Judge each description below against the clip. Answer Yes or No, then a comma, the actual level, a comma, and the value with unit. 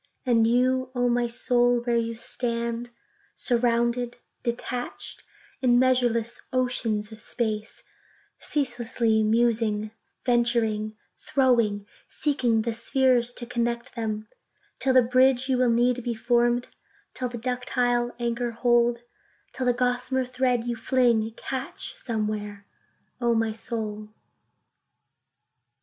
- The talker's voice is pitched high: Yes, high, 240 Hz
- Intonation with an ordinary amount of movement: No, narrow, 1.5 semitones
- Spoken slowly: Yes, slow, 100 wpm